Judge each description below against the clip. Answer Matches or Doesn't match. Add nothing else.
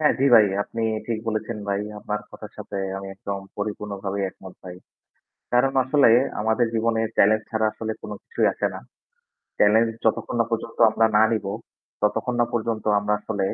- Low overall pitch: Matches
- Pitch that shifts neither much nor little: Doesn't match